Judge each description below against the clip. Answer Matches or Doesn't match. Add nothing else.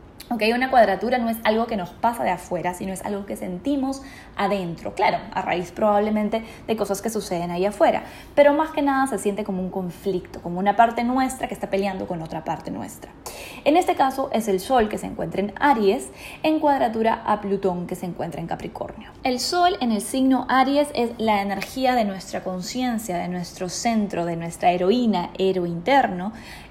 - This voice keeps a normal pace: Doesn't match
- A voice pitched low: Doesn't match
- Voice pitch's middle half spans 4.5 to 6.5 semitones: Matches